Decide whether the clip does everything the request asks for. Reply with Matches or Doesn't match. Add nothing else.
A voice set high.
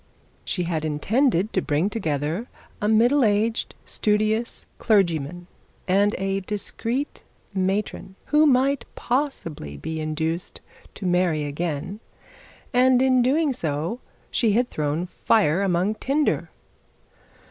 Matches